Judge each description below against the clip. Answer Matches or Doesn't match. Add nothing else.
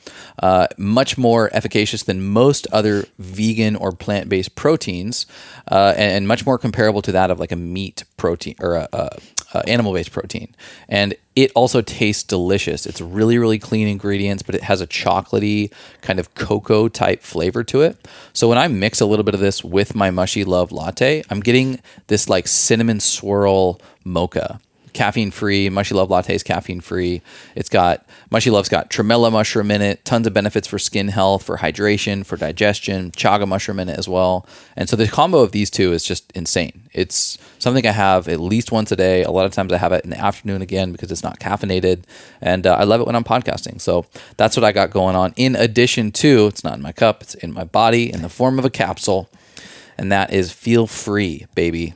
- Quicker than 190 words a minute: Matches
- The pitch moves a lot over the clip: Doesn't match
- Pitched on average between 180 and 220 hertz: Doesn't match